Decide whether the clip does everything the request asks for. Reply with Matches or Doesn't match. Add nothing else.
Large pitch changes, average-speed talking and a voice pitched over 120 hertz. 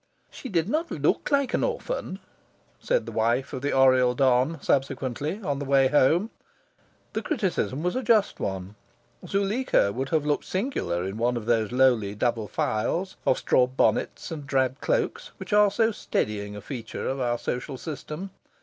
Matches